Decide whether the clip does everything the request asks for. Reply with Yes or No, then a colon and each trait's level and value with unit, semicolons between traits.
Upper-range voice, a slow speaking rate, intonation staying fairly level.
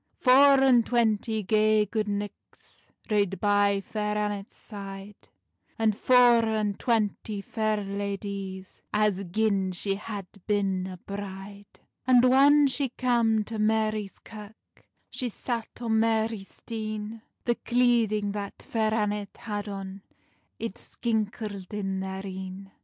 Yes: high, 210 Hz; slow, 125 wpm; narrow, 2.2 semitones